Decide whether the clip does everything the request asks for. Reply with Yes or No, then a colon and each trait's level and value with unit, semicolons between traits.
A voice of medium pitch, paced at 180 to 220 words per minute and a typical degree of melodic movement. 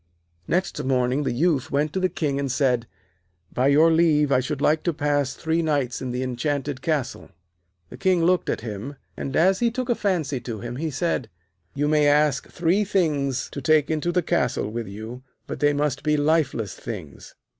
Yes: medium, 145 Hz; average, 195 wpm; average, 4.1 semitones